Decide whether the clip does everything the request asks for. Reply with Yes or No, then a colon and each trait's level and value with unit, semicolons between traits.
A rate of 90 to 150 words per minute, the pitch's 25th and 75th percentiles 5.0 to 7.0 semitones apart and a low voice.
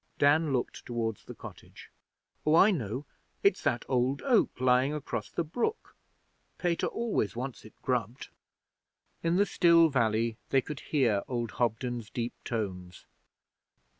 Yes: slow, 135 wpm; wide, 5.4 semitones; low, 130 Hz